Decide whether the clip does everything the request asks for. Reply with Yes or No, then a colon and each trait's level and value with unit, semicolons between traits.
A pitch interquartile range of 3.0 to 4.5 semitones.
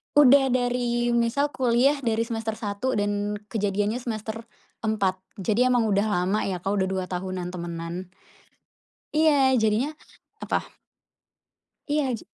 Yes: average, 4.0 semitones